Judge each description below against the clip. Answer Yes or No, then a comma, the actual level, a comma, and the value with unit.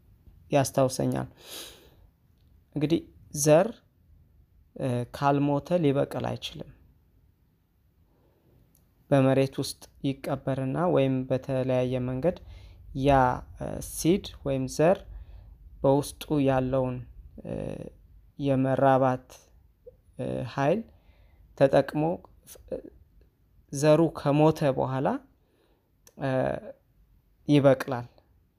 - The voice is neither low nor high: No, low, 130 Hz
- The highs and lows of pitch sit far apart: Yes, wide, 7.4 semitones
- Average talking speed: No, slow, 50 wpm